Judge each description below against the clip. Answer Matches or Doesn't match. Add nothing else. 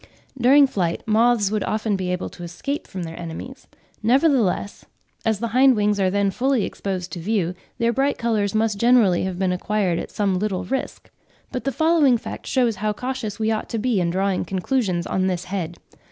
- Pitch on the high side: Matches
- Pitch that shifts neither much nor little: Matches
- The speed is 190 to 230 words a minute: Matches